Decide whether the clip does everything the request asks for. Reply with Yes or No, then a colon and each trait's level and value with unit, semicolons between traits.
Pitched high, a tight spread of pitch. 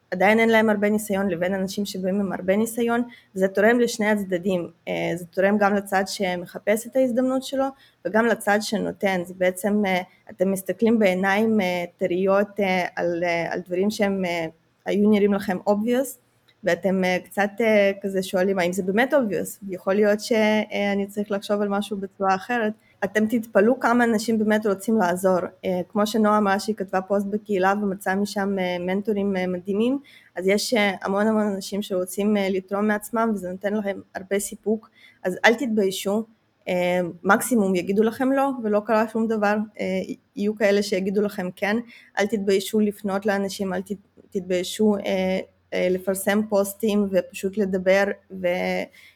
Yes: high, 200 Hz; narrow, 2.2 semitones